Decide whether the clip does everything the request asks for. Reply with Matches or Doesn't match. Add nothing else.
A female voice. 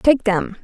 Matches